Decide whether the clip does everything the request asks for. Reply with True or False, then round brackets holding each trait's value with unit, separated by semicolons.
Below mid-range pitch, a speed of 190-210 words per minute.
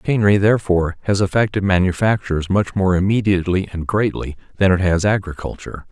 False (95 Hz; 140 wpm)